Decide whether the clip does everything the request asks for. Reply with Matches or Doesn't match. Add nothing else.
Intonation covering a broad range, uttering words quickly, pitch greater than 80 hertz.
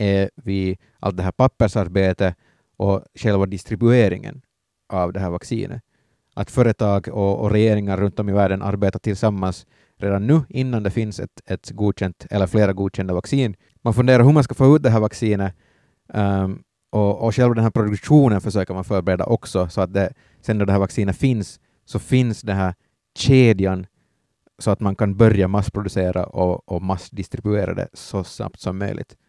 Doesn't match